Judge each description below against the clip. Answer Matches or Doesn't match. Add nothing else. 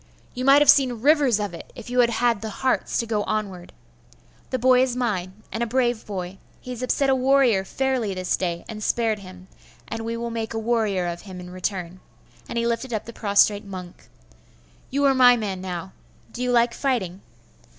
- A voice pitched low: Doesn't match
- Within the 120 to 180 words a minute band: Doesn't match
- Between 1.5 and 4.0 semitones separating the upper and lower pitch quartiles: Doesn't match